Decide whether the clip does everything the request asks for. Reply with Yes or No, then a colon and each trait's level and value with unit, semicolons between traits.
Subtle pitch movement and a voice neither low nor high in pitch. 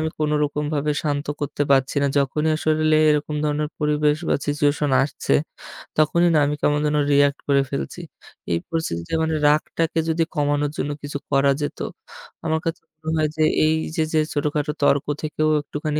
Yes: narrow, 1.2 semitones; medium, 150 Hz